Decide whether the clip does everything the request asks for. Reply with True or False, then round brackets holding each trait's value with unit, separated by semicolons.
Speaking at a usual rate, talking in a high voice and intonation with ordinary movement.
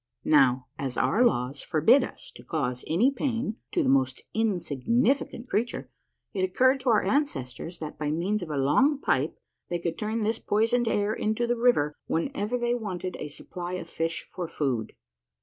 False (175 wpm; 195 Hz; 7.8 semitones)